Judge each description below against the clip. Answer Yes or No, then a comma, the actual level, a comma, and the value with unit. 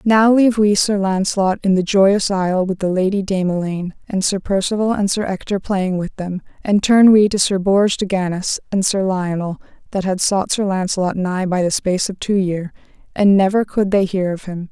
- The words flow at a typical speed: No, fast, 215 wpm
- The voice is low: No, high, 195 Hz